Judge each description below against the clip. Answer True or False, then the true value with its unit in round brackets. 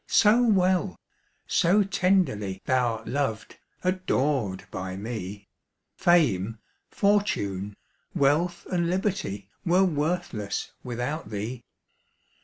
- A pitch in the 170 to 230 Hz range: False (145 Hz)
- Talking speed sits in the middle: False (85 wpm)